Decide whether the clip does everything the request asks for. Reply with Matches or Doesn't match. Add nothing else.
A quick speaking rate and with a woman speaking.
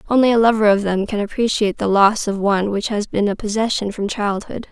Matches